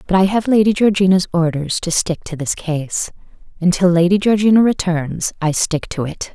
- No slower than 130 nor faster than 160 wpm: No, average, 190 wpm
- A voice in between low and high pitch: Yes, medium, 180 Hz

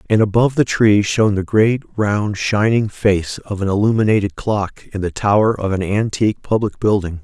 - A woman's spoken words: No, male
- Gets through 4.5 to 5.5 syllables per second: Yes, 5.0 syllables/s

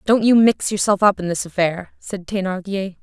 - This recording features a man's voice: No, female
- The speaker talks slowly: No, average, 200 wpm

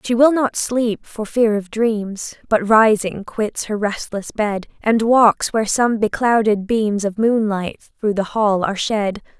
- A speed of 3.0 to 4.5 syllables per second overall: Yes, 3.9 syllables/s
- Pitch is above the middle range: Yes, high, 215 Hz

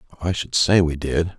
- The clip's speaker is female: No, male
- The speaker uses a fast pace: Yes, fast, 215 wpm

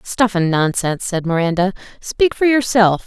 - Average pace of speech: Yes, average, 155 wpm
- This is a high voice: Yes, high, 200 Hz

